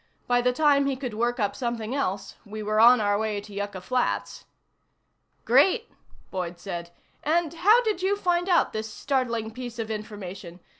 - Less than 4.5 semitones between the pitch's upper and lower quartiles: No, average, 5.3 semitones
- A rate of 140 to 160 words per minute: No, average, 170 wpm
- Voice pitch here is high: Yes, high, 230 Hz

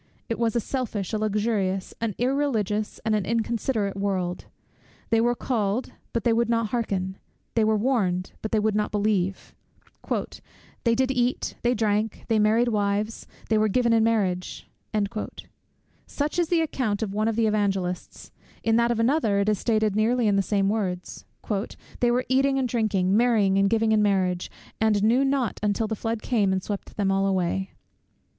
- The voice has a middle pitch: No, high, 215 Hz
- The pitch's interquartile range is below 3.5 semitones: Yes, average, 2.8 semitones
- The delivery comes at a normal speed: Yes, average, 180 wpm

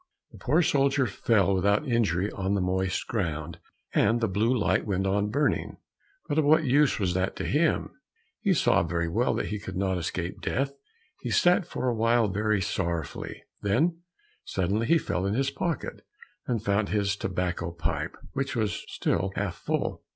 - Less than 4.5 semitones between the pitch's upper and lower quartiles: No, wide, 5.5 semitones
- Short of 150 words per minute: No, average, 175 wpm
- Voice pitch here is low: Yes, low, 105 Hz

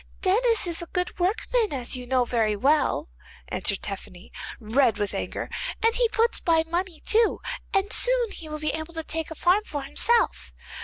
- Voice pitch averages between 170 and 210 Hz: No, very high, 325 Hz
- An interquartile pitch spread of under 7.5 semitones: No, wide, 8.1 semitones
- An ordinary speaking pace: Yes, average, 185 wpm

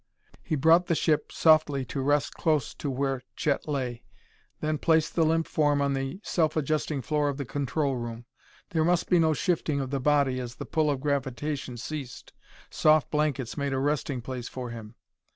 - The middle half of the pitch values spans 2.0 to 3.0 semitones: Yes, average, 2.7 semitones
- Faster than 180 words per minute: Yes, average, 190 wpm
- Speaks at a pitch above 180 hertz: No, medium, 145 Hz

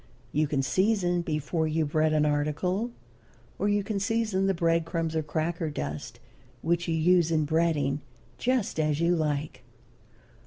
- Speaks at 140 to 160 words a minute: Yes, average, 155 wpm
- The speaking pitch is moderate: Yes, medium, 165 Hz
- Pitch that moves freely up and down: No, average, 3.1 semitones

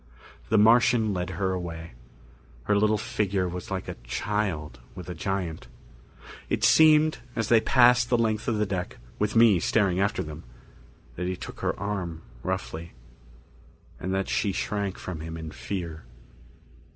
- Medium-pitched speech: No, very low, 95 Hz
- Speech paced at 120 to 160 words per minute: Yes, average, 155 wpm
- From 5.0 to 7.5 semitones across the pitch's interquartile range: No, average, 3.8 semitones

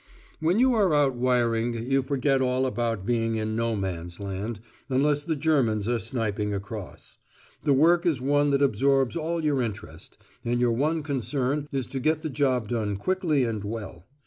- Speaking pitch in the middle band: No, low, 125 Hz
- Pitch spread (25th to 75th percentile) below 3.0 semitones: No, average, 4.5 semitones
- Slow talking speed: No, average, 175 wpm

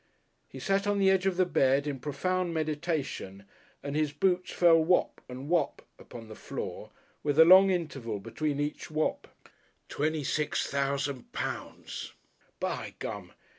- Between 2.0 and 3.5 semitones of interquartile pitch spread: No, average, 4.3 semitones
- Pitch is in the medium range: Yes, medium, 155 Hz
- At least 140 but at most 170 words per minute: Yes, average, 150 wpm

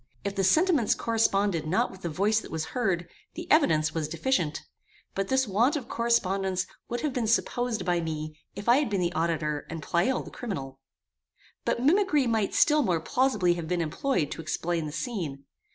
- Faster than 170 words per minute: Yes, average, 185 wpm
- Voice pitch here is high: Yes, high, 195 Hz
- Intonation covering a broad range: Yes, wide, 6.8 semitones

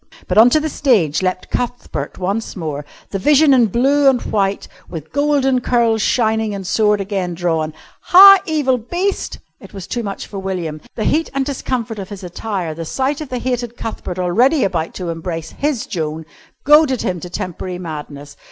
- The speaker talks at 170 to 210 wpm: Yes, average, 185 wpm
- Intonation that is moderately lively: No, wide, 6.5 semitones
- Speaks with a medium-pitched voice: No, high, 210 Hz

